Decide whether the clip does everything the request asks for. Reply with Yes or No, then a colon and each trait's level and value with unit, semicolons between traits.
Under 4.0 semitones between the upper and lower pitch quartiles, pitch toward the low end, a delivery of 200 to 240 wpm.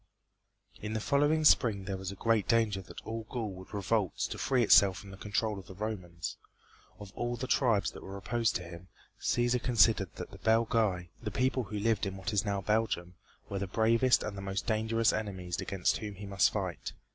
Yes: average, 2.8 semitones; low, 105 Hz; fast, 205 wpm